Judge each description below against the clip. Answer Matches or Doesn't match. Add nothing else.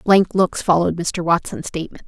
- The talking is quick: Doesn't match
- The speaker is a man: Doesn't match